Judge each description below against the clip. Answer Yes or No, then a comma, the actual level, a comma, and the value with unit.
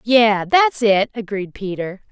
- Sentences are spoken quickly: No, average, 140 wpm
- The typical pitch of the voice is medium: No, high, 215 Hz